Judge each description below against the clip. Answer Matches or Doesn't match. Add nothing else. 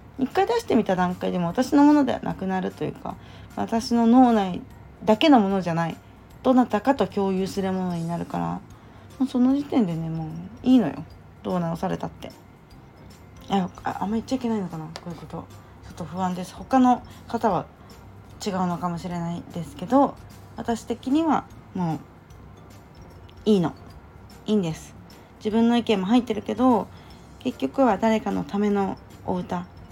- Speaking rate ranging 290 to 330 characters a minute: Matches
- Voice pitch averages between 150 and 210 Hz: Matches